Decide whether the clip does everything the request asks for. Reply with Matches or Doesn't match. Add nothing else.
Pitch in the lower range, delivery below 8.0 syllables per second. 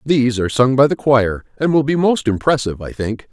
Matches